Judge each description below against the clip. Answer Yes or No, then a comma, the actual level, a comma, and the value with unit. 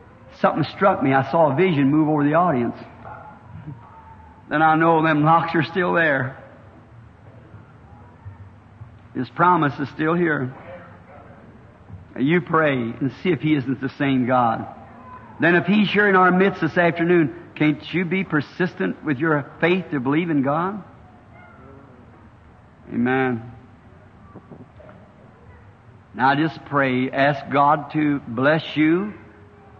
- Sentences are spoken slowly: Yes, slow, 130 wpm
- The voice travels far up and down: Yes, wide, 5.9 semitones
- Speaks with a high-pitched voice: No, low, 135 Hz